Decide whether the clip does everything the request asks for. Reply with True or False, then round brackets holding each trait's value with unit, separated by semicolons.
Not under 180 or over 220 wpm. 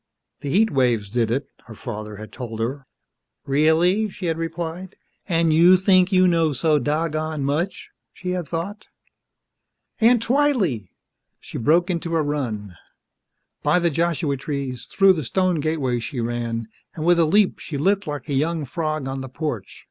False (165 wpm)